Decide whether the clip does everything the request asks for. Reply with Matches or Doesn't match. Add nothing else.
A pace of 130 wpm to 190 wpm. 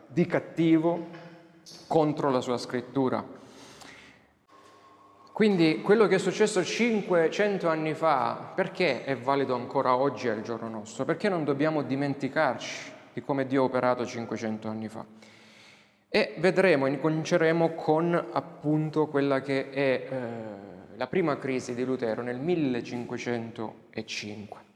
Doesn't match